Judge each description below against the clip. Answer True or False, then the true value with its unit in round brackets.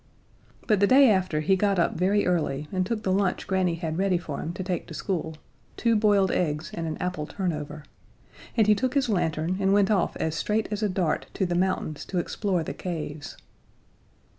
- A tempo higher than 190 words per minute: True (205 wpm)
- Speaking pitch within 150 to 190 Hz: True (185 Hz)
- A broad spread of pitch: False (3.8 semitones)